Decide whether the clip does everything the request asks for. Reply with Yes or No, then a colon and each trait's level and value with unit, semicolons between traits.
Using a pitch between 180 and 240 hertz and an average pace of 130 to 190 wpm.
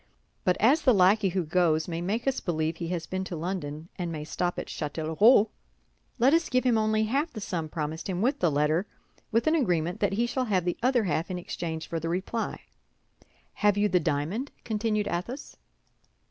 No: medium, 185 Hz; average, 200 wpm